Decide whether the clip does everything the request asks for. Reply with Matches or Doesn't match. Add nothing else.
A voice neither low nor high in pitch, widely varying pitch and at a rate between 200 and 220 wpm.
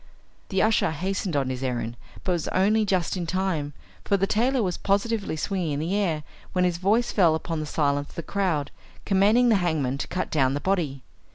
Doesn't match